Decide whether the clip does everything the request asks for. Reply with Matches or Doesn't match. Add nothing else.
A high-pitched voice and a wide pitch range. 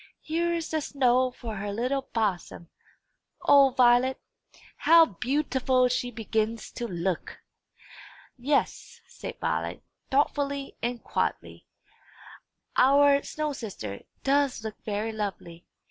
Doesn't match